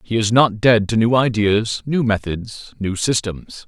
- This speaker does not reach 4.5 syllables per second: Yes, 4.0 syllables/s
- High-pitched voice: No, low, 110 Hz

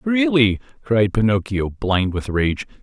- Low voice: Yes, low, 115 Hz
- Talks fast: No, slow, 125 wpm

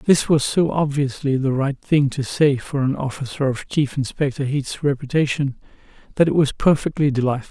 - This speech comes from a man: Yes, male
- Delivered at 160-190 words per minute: Yes, average, 175 wpm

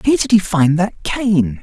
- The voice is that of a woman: No, male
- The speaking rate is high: Yes, fast, 220 wpm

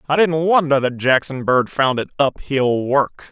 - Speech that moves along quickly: No, average, 180 wpm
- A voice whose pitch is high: No, medium, 140 Hz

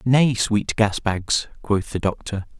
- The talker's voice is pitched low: Yes, low, 105 Hz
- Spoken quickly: No, average, 160 wpm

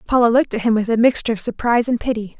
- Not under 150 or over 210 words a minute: No, fast, 275 wpm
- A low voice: No, high, 230 Hz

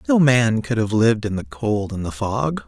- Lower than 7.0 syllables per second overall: Yes, 4.8 syllables/s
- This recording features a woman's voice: No, male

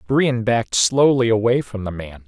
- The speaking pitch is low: Yes, low, 115 Hz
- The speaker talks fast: No, average, 185 wpm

